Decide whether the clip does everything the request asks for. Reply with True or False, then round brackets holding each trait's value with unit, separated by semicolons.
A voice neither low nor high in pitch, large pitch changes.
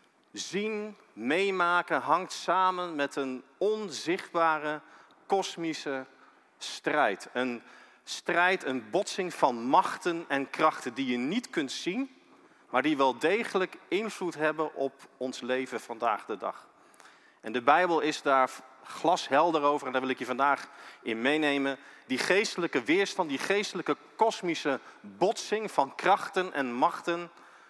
True (160 Hz; 5.7 semitones)